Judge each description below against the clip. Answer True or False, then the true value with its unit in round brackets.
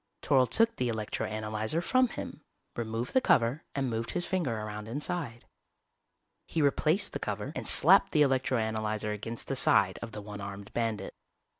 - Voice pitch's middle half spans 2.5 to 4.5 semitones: False (5.2 semitones)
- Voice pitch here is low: True (115 Hz)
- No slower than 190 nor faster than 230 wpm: False (170 wpm)